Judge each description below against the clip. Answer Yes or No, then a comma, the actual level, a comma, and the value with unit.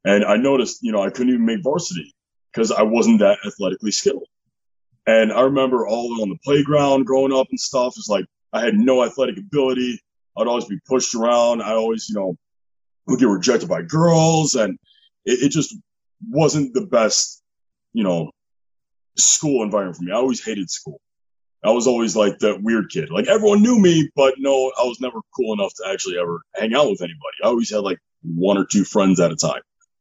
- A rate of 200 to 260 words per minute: Yes, fast, 205 wpm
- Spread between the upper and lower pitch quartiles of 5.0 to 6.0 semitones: Yes, wide, 5.6 semitones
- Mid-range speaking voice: No, low, 130 Hz